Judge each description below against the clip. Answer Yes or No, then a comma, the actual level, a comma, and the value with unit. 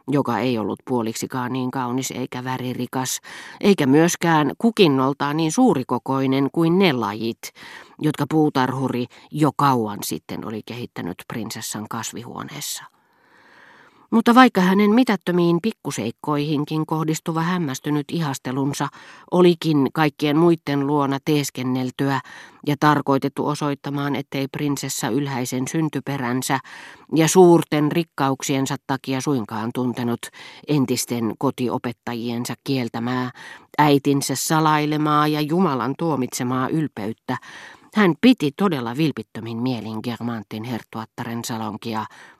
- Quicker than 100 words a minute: No, slow, 95 wpm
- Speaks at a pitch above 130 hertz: Yes, medium, 140 Hz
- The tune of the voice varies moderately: Yes, average, 3.6 semitones